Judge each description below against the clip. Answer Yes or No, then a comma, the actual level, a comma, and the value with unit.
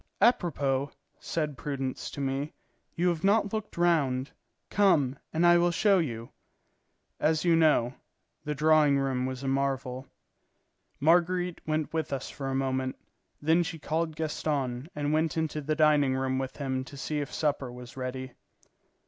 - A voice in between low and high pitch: Yes, medium, 145 Hz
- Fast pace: No, average, 155 wpm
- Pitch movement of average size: Yes, average, 3.4 semitones